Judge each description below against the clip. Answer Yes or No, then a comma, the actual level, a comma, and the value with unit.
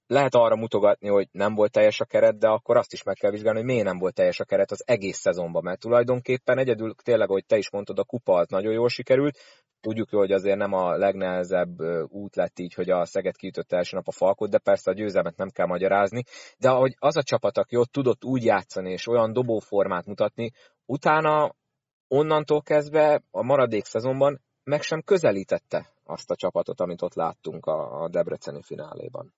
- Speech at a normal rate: No, fast, 195 wpm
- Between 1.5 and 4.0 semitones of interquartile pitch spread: No, wide, 5.8 semitones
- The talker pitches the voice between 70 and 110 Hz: No, low, 120 Hz